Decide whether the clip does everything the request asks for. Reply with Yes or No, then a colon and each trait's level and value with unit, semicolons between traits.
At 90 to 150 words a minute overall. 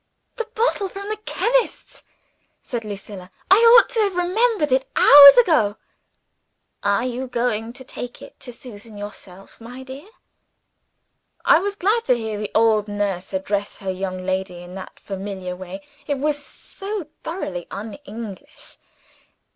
Yes: average, 145 wpm